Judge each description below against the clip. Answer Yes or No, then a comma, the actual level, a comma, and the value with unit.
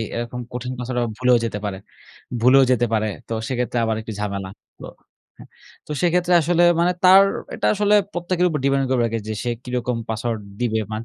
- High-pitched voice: No, low, 125 Hz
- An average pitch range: No, wide, 6.3 semitones